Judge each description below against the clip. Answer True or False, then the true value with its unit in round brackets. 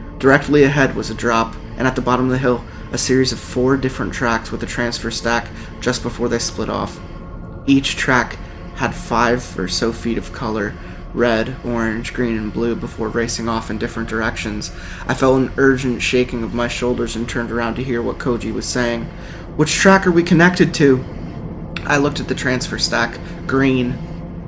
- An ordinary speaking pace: True (190 wpm)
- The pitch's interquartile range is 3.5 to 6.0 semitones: False (2.5 semitones)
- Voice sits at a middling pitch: False (120 Hz)